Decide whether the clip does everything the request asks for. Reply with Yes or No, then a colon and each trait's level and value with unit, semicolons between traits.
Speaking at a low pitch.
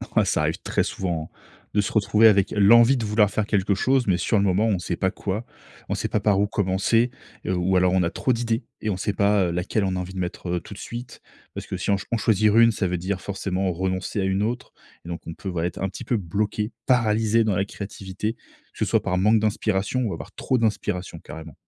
Yes: low, 100 Hz